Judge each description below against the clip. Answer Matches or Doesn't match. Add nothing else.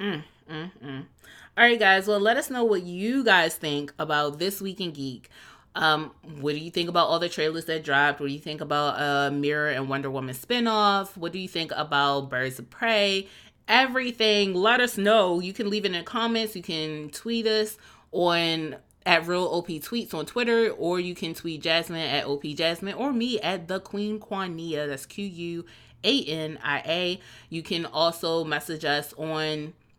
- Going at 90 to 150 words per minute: Doesn't match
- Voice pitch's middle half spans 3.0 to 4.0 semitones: Doesn't match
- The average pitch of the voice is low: Doesn't match